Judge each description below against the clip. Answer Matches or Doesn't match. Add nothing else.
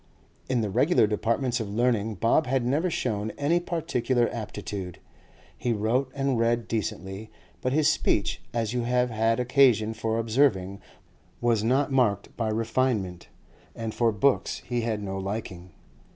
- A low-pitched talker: Matches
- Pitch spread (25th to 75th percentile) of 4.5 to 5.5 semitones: Doesn't match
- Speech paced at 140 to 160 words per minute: Matches